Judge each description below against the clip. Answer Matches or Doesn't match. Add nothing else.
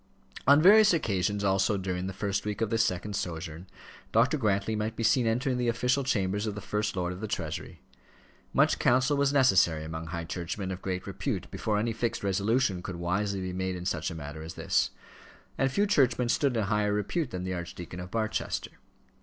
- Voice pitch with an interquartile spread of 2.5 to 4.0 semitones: Doesn't match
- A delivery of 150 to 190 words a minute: Doesn't match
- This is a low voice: Matches